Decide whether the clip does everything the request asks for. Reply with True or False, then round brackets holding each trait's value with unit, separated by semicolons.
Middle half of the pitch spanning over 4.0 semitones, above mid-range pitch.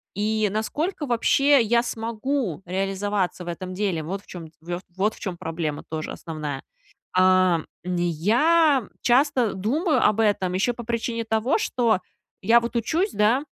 True (4.7 semitones; 210 Hz)